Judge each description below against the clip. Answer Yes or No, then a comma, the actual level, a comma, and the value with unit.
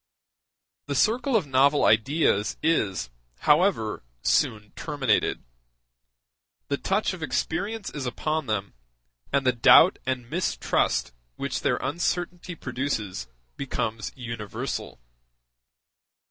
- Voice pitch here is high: No, medium, 140 Hz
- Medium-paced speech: No, slow, 100 wpm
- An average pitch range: No, wide, 6.9 semitones